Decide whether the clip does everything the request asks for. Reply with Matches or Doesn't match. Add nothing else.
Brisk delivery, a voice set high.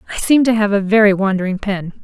Matches